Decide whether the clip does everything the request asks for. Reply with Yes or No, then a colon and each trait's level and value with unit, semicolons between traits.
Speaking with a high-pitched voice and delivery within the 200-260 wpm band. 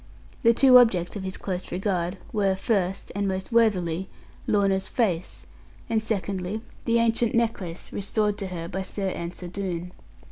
No: high, 195 Hz; average, 150 wpm